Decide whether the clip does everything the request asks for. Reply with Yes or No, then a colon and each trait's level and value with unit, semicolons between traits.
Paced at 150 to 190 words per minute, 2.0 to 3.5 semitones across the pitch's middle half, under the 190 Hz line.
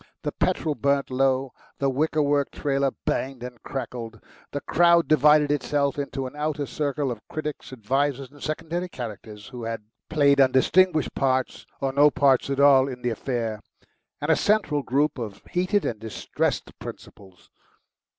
Yes: average, 155 wpm; average, 2.8 semitones; medium, 140 Hz